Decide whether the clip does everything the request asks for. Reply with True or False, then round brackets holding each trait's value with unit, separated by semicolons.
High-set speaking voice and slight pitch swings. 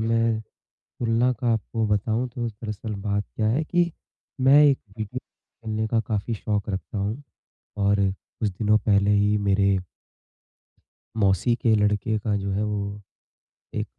False (110 Hz; 2.1 semitones)